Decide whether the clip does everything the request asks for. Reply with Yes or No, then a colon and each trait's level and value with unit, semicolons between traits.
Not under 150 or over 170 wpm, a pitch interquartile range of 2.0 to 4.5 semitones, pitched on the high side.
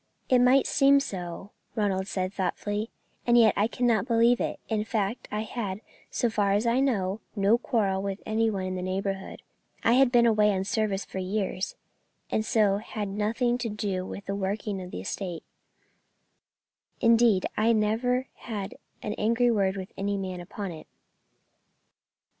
Yes: average, 165 wpm; average, 3.1 semitones; high, 210 Hz